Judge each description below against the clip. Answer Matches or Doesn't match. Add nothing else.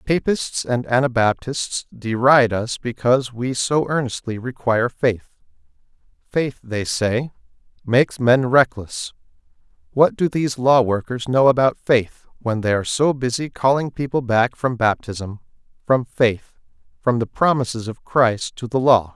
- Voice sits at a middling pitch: Doesn't match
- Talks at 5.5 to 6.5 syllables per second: Doesn't match